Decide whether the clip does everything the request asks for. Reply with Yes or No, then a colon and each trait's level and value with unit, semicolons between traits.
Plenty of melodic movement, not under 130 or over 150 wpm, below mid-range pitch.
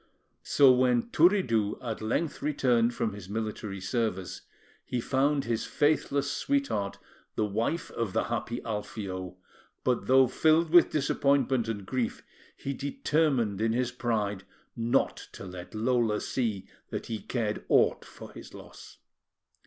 No: average, 4.3 semitones; slow, 135 wpm; low, 120 Hz